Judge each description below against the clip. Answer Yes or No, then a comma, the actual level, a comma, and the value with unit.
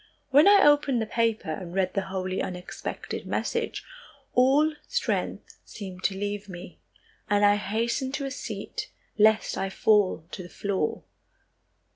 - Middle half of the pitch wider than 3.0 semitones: Yes, wide, 5.4 semitones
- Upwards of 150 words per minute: No, average, 145 wpm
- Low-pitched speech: No, high, 205 Hz